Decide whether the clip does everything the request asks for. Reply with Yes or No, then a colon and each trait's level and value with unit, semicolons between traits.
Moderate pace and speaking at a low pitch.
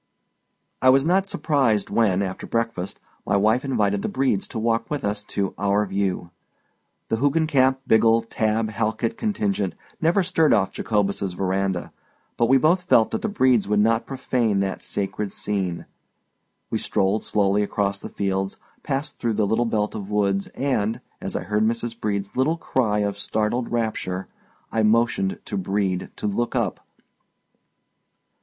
Yes: average, 155 wpm; low, 110 Hz